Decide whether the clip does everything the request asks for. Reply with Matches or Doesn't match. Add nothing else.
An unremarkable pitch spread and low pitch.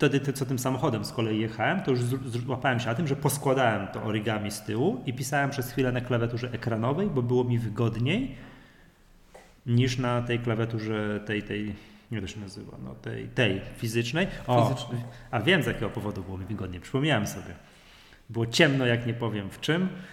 Matches